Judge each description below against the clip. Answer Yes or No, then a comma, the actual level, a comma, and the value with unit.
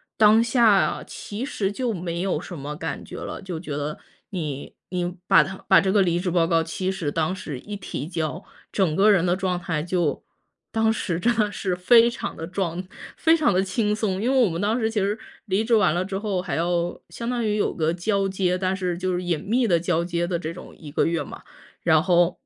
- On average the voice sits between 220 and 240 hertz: No, medium, 185 Hz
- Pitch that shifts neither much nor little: Yes, average, 3.5 semitones